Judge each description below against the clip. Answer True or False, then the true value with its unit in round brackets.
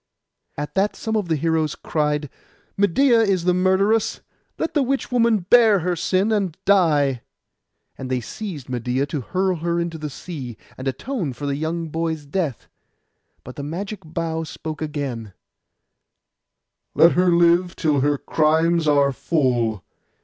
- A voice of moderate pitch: True (165 Hz)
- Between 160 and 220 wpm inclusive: False (150 wpm)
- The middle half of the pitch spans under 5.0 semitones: True (4.6 semitones)